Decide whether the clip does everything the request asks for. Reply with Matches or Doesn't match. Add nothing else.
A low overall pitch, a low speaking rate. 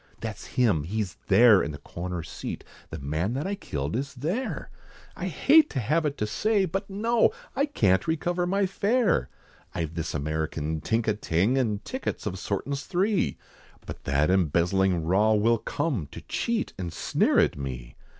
Doesn't match